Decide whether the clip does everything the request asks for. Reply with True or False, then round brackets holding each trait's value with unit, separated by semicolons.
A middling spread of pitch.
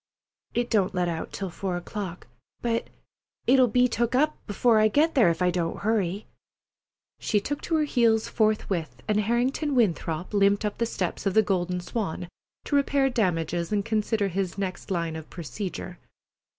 True (4.8 semitones)